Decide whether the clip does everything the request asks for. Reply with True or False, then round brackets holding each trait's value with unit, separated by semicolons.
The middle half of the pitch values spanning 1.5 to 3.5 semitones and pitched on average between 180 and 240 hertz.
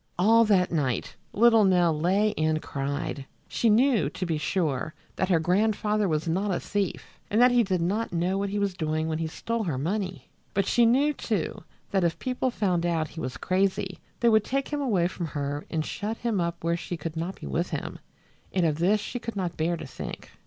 False (4.7 semitones; 185 Hz)